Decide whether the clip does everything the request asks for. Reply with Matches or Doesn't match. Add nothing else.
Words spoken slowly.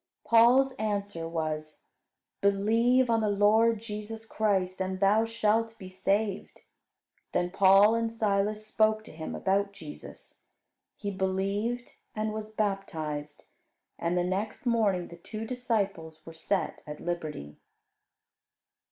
Matches